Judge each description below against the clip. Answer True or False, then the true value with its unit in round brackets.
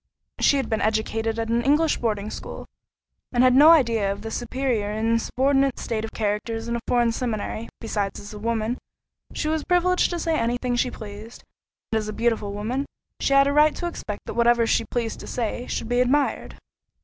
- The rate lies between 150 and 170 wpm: False (200 wpm)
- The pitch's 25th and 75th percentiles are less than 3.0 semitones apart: False (3.4 semitones)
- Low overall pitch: False (235 Hz)